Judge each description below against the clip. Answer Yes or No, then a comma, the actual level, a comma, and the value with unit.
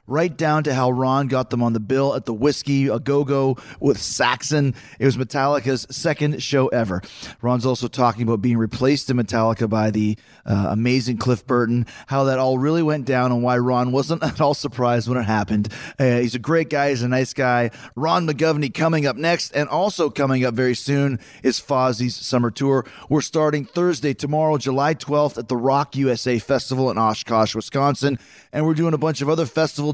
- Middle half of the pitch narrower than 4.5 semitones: Yes, average, 3.0 semitones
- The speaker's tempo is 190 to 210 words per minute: Yes, average, 200 wpm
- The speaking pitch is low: Yes, low, 130 Hz